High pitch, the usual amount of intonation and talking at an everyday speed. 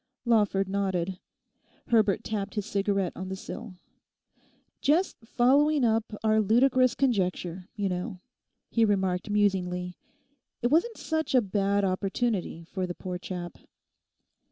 No: high, 200 Hz; average, 3.9 semitones; slow, 125 wpm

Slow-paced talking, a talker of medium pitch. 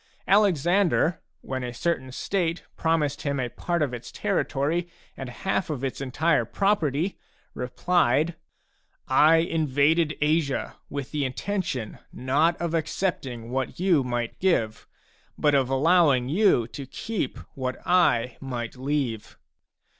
Yes: slow, 125 wpm; medium, 145 Hz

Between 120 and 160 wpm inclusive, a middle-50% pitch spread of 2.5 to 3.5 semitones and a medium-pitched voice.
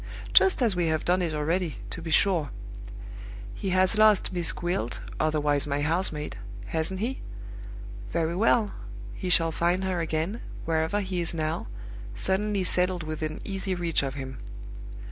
Yes: average, 155 wpm; average, 3.2 semitones; medium, 170 Hz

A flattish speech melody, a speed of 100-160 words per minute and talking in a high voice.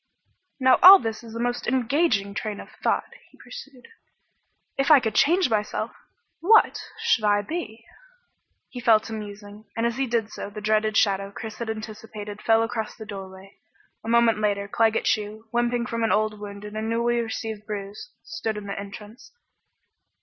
No: narrow, 2.2 semitones; average, 175 wpm; high, 220 Hz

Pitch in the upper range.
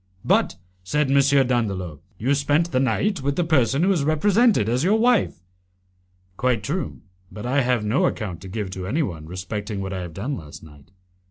No: low, 125 Hz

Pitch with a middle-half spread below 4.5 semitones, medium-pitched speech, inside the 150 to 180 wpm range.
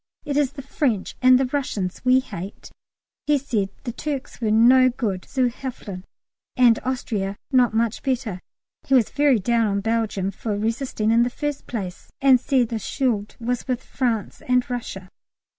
No: average, 3.5 semitones; high, 240 Hz; average, 170 wpm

